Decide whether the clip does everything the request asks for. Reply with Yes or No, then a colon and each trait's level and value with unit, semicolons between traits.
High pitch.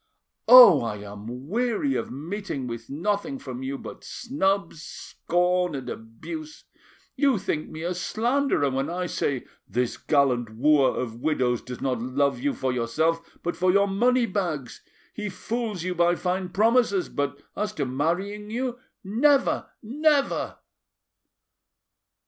No: medium, 175 Hz